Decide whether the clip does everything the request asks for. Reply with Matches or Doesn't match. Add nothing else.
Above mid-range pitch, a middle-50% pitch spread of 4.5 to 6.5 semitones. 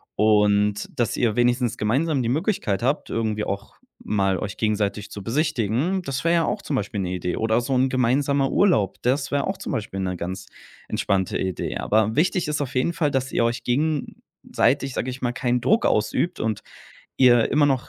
Doesn't match